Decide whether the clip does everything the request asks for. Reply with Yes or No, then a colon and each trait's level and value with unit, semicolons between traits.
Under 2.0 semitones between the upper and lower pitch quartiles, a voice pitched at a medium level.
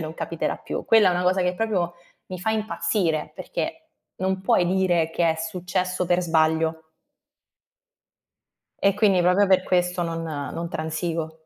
No: narrow, 2.4 semitones; medium, 180 Hz